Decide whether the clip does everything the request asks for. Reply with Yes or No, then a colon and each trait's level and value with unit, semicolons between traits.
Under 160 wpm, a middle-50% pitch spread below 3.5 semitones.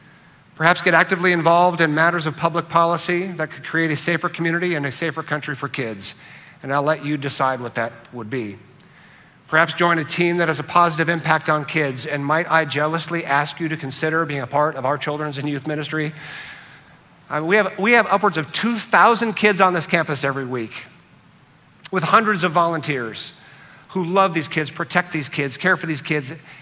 No: average, 200 wpm; average, 2.9 semitones